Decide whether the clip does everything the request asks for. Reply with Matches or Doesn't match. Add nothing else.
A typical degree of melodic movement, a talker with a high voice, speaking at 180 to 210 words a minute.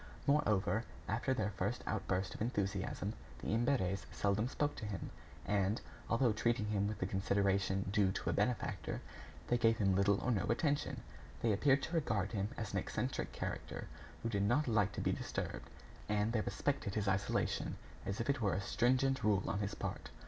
Doesn't match